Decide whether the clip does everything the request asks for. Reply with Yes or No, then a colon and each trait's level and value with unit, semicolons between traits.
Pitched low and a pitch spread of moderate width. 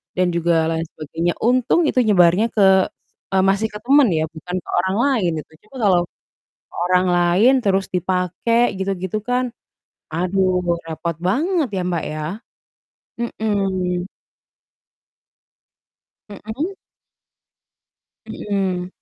No: high, 190 Hz; average, 3.9 semitones